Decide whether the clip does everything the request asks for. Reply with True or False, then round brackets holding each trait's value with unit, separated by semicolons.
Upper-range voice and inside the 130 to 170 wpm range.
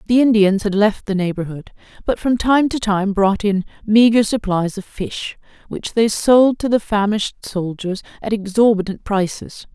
True (210 Hz; 165 wpm)